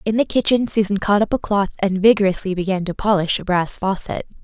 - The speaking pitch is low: No, high, 200 Hz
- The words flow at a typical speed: No, fast, 215 wpm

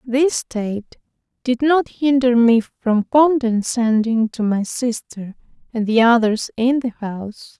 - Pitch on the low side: No, high, 235 Hz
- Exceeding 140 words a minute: No, slow, 135 wpm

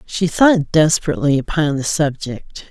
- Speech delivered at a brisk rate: No, slow, 135 wpm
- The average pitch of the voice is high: No, medium, 155 Hz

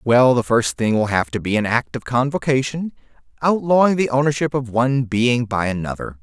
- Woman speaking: No, male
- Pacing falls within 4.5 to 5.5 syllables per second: Yes, 5.3 syllables/s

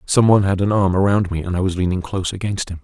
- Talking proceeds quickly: Yes, fast, 295 wpm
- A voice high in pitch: No, very low, 95 Hz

